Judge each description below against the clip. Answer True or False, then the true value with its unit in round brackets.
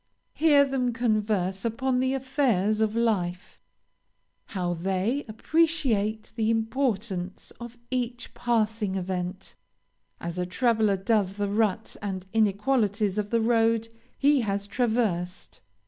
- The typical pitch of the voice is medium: False (220 Hz)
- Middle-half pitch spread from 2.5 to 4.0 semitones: True (3.7 semitones)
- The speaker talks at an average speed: False (115 wpm)